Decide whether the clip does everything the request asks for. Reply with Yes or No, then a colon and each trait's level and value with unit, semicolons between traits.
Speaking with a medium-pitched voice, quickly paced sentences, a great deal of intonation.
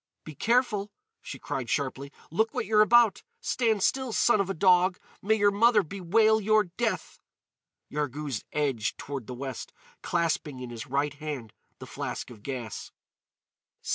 No: medium, 175 Hz; average, 150 wpm; wide, 7.7 semitones